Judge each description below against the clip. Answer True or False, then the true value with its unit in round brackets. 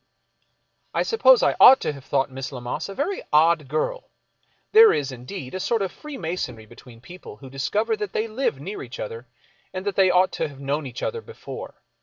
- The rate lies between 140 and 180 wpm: False (200 wpm)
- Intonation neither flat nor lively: False (8.0 semitones)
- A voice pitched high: False (160 Hz)